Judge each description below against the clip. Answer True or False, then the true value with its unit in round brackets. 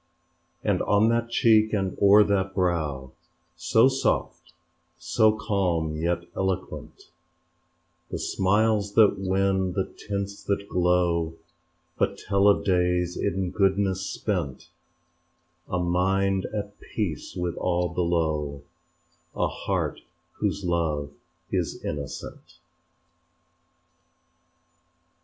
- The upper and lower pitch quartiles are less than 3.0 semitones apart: True (2.6 semitones)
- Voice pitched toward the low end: True (95 Hz)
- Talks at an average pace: False (100 wpm)